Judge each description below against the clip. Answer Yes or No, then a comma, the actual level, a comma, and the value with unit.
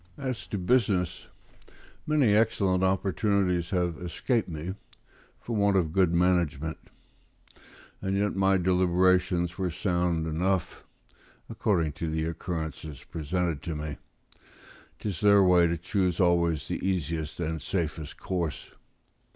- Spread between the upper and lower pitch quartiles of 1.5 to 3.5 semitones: Yes, average, 2.7 semitones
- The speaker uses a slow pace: Yes, slow, 120 wpm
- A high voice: No, very low, 90 Hz